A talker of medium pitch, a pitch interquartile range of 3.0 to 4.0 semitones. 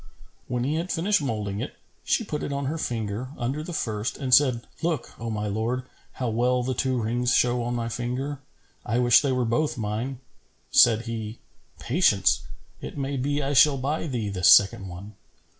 No: low, 125 Hz; average, 3.7 semitones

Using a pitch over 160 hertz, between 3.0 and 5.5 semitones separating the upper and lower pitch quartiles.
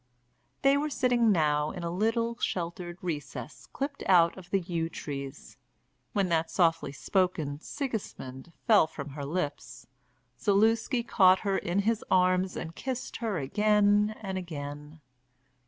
Yes: medium, 185 Hz; average, 5.0 semitones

